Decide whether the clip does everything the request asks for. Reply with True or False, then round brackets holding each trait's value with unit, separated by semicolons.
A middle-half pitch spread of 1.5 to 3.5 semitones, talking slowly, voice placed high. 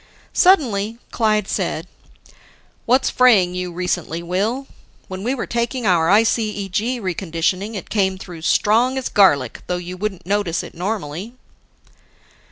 False (4.2 semitones; 130 wpm; 200 Hz)